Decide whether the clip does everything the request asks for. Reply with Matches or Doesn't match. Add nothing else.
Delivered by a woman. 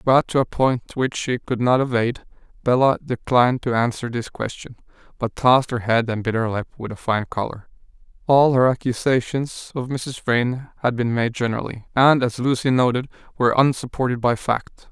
Doesn't match